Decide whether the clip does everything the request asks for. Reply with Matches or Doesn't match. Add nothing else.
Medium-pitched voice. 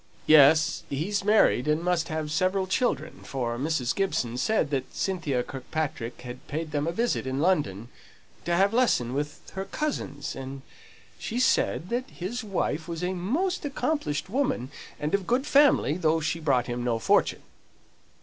Matches